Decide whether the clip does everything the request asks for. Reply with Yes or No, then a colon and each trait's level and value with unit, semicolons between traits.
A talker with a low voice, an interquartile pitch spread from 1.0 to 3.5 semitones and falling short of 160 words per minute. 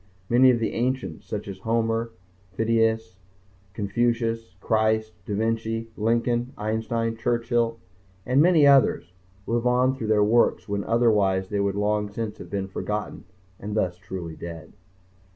Yes: low, 110 Hz; narrow, 2.4 semitones; average, 145 wpm